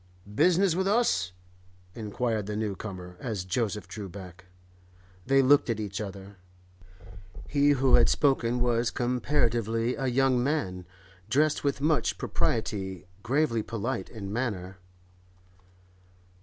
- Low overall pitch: Yes, low, 115 Hz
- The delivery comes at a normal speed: No, slow, 120 wpm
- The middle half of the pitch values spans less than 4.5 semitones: No, average, 5.2 semitones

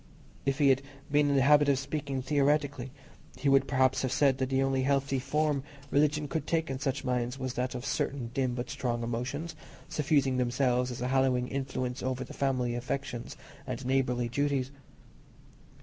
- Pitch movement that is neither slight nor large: No, narrow, 1.9 semitones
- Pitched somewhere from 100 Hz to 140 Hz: Yes, low, 135 Hz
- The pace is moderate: Yes, average, 180 wpm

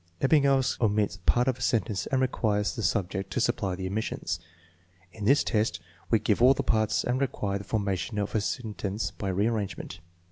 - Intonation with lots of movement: No, average, 3.4 semitones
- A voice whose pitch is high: No, low, 105 Hz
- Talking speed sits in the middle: Yes, average, 180 wpm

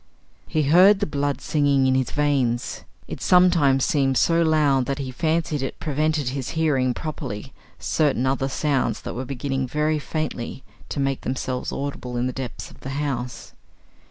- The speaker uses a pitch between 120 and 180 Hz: Yes, medium, 140 Hz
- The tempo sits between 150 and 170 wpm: Yes, average, 165 wpm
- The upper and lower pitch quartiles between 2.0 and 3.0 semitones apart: Yes, average, 2.7 semitones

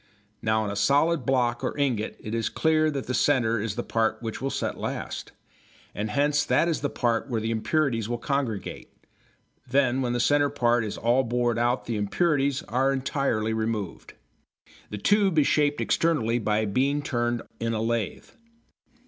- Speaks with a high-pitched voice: No, low, 120 Hz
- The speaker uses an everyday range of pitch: Yes, average, 4.0 semitones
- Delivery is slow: No, average, 175 wpm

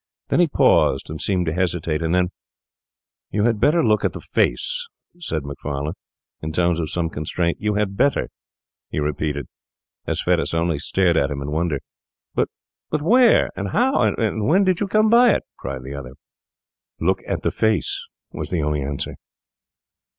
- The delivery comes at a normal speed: Yes, average, 170 wpm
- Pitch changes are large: Yes, wide, 7.7 semitones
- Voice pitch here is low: Yes, very low, 85 Hz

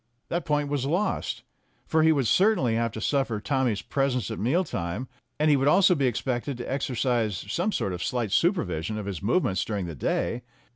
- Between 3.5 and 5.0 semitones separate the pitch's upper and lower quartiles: No, wide, 5.4 semitones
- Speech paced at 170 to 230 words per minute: Yes, average, 195 wpm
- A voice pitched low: Yes, low, 130 Hz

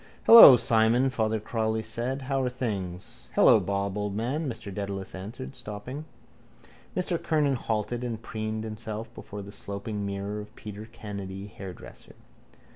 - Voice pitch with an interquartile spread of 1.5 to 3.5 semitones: Yes, average, 3.2 semitones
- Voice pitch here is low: Yes, low, 110 Hz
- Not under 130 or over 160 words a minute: Yes, average, 140 wpm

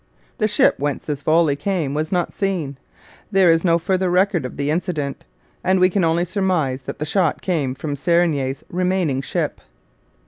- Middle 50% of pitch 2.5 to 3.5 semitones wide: No, average, 4.3 semitones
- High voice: No, medium, 165 Hz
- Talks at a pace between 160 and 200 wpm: Yes, average, 175 wpm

